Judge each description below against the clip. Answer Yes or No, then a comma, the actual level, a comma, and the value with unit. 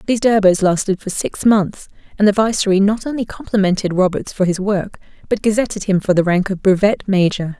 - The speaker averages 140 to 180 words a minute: No, average, 195 wpm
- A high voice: Yes, high, 200 Hz